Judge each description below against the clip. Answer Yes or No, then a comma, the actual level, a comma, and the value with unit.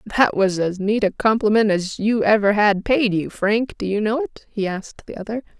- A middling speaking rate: No, fast, 225 wpm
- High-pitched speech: Yes, high, 210 Hz